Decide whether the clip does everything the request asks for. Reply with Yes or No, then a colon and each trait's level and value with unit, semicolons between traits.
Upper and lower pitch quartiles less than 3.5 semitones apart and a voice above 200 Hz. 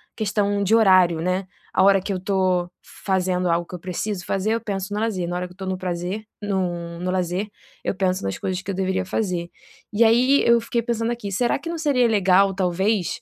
No: average, 2.9 semitones; high, 190 Hz